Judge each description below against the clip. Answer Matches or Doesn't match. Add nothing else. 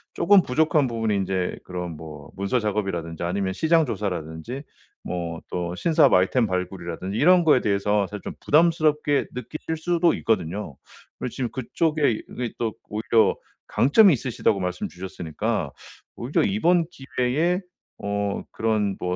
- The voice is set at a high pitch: Doesn't match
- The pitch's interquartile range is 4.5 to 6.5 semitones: Doesn't match